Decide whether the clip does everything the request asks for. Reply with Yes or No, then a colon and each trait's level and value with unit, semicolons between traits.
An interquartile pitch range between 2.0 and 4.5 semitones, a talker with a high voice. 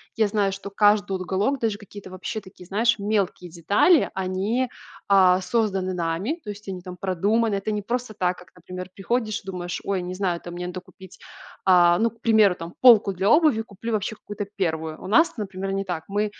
Yes: average, 2.8 semitones; high, 195 Hz